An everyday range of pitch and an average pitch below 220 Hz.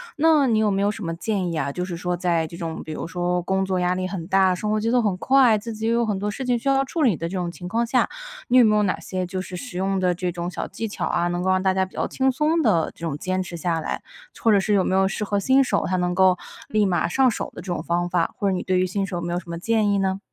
Yes: average, 3.5 semitones; high, 190 Hz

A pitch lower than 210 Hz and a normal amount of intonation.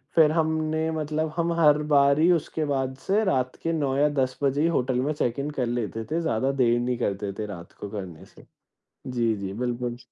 Yes: low, 135 Hz; average, 4.6 semitones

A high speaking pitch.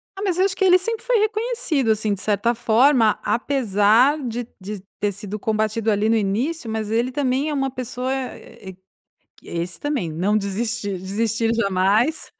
Yes: high, 230 Hz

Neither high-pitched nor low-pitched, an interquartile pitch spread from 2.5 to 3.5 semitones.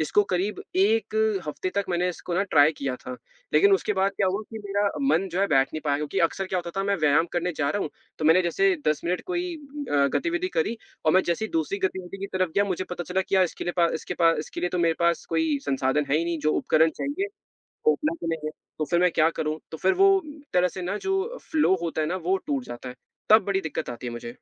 No: medium, 180 Hz; average, 4.5 semitones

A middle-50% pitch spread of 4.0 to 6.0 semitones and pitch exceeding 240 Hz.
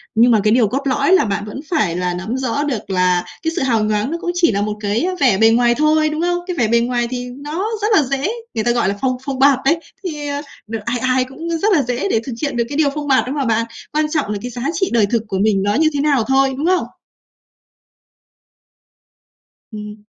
Yes: average, 5.3 semitones; very high, 255 Hz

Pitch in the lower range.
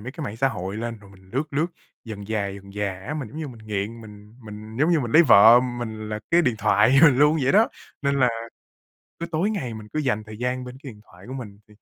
Yes: low, 115 Hz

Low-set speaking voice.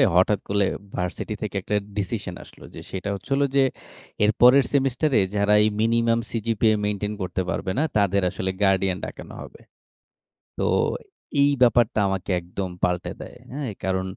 Yes: low, 105 Hz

